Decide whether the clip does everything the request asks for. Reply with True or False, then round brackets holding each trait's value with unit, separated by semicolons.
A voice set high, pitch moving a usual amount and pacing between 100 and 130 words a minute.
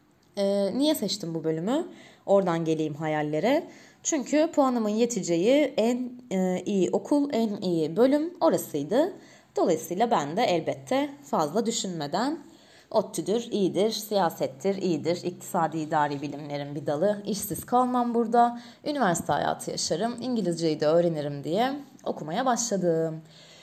False (205 Hz; 6.8 semitones; 110 wpm)